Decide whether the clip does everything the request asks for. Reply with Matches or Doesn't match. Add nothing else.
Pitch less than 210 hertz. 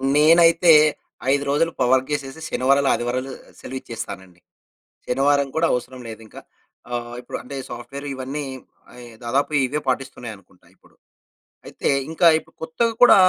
Matches